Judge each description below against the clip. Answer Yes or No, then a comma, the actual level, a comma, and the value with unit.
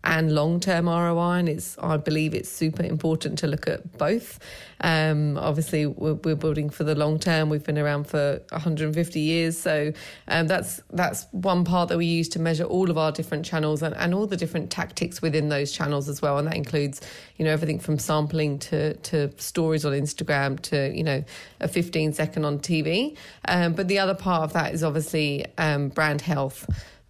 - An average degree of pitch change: No, narrow, 1.8 semitones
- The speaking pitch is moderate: Yes, medium, 155 Hz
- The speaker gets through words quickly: No, average, 190 wpm